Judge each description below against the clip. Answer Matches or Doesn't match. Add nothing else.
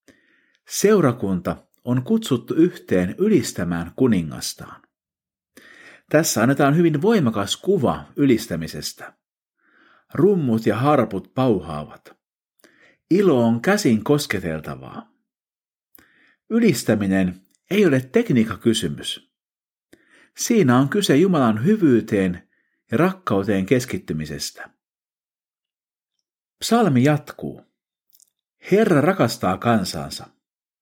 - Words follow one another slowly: Matches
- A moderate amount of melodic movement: Doesn't match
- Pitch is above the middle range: Doesn't match